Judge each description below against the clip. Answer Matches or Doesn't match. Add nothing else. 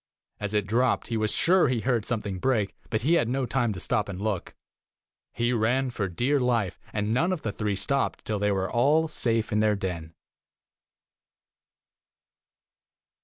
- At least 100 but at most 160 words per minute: Doesn't match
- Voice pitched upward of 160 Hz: Doesn't match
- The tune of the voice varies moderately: Matches